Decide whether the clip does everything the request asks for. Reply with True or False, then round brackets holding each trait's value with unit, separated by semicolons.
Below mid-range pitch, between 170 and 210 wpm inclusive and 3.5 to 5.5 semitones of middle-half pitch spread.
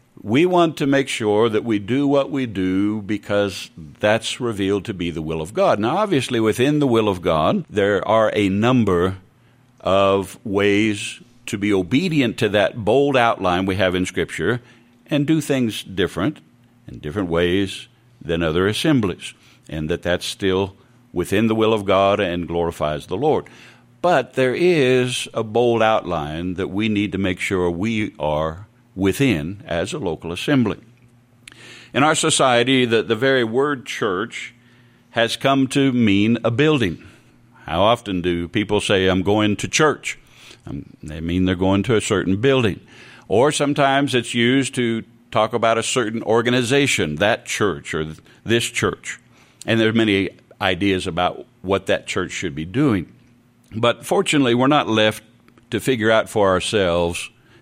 False (110 Hz; 160 wpm; 4.4 semitones)